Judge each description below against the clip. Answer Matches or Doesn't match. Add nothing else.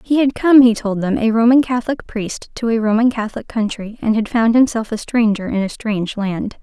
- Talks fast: Matches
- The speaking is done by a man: Doesn't match